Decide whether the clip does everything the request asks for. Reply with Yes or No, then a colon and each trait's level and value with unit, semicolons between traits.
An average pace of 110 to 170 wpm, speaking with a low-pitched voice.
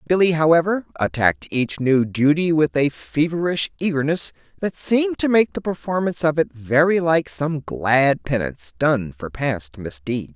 No: average, 155 wpm; medium, 145 Hz